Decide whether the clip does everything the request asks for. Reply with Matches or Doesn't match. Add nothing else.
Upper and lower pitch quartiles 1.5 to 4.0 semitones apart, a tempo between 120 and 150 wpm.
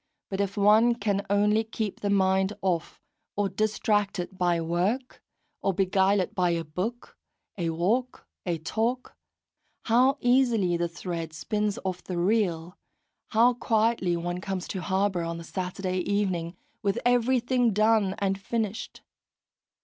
Matches